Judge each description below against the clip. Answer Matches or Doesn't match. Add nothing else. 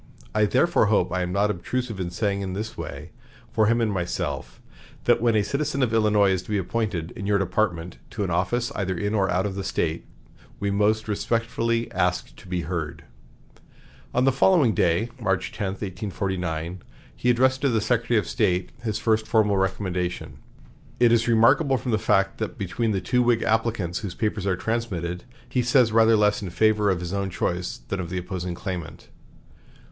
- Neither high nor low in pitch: Doesn't match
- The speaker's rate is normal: Matches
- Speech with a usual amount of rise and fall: Matches